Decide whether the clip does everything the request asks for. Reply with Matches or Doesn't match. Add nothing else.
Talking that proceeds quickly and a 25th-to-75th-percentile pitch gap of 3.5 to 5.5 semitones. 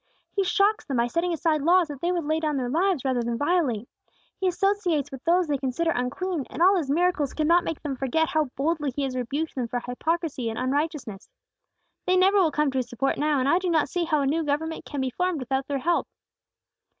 Matches